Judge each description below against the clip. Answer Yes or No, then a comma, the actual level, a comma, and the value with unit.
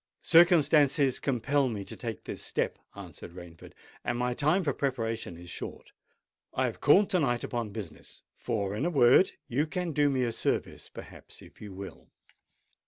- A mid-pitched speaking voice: No, low, 125 Hz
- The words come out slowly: No, average, 170 wpm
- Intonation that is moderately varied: No, wide, 5.7 semitones